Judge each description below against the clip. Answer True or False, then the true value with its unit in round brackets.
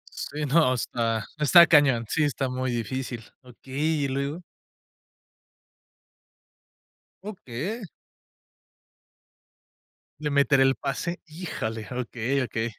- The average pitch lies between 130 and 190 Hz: True (135 Hz)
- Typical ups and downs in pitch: True (3.8 semitones)